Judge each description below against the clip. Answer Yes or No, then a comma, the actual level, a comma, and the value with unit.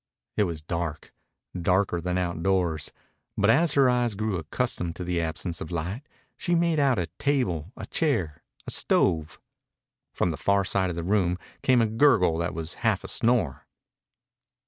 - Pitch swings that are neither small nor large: No, wide, 5.7 semitones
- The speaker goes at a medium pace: Yes, average, 170 wpm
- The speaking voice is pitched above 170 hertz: No, very low, 90 Hz